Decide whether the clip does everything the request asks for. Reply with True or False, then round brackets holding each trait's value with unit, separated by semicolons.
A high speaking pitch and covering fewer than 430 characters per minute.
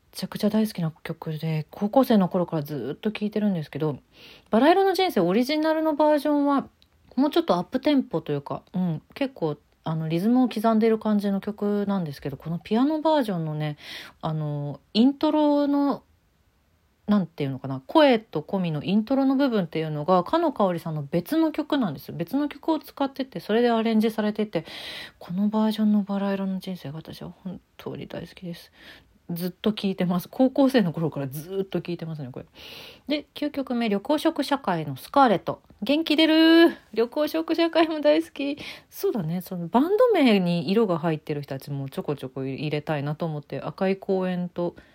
True (200 Hz; 385 characters per minute)